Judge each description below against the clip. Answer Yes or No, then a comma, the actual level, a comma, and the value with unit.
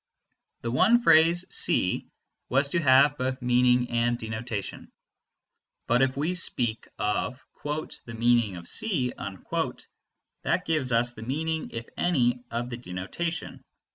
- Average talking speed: No, slow, 130 wpm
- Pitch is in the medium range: No, low, 125 Hz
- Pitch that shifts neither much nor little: Yes, average, 4.4 semitones